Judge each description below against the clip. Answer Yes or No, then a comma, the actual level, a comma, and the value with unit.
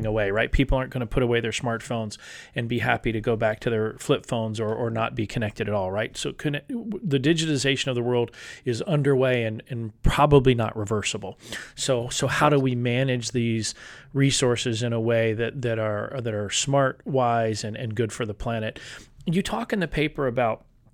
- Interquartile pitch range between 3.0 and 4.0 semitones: Yes, average, 3.4 semitones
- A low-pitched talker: Yes, low, 120 Hz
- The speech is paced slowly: No, fast, 205 wpm